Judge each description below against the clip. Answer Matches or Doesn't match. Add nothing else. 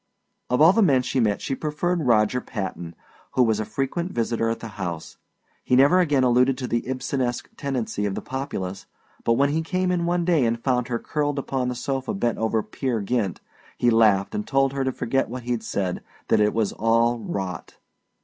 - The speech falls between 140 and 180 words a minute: Doesn't match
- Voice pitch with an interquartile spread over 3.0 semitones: Matches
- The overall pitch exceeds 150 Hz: Doesn't match